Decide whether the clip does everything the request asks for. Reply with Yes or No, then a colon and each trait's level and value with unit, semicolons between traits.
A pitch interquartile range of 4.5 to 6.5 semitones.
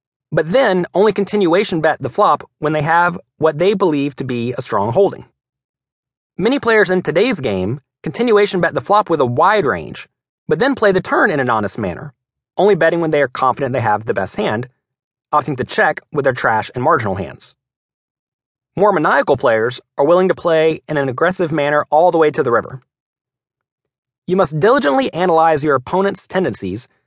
Yes: wide, 5.6 semitones